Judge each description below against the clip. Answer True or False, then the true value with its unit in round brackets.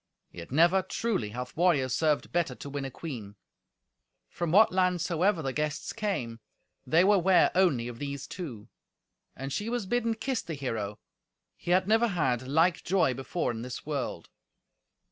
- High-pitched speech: False (160 Hz)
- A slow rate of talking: False (165 wpm)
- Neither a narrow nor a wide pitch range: False (6.4 semitones)